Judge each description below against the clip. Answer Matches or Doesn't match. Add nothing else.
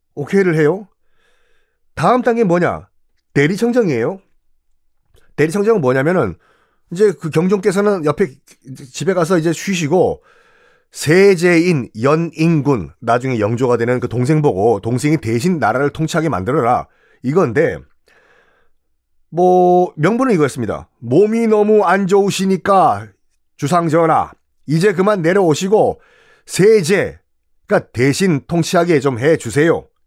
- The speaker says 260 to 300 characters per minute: Matches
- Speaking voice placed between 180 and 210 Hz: Doesn't match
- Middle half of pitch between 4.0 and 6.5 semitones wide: Doesn't match